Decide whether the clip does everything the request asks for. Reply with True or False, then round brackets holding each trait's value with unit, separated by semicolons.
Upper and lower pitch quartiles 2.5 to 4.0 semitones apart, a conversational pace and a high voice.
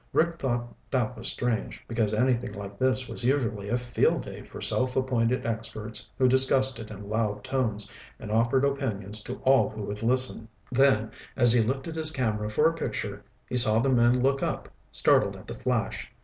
False (3.3 semitones; 190 wpm; 120 Hz)